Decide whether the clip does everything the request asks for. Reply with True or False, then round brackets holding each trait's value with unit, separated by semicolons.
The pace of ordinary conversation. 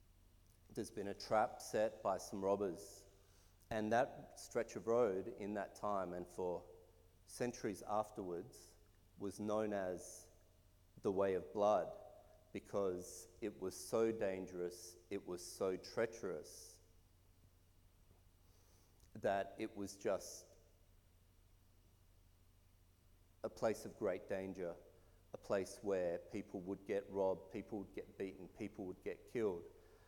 False (120 wpm)